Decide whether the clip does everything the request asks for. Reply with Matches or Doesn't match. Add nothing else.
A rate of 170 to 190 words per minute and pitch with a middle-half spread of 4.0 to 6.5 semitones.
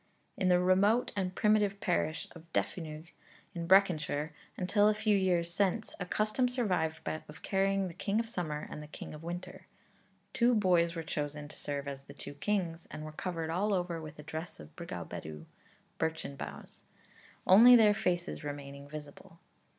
Matches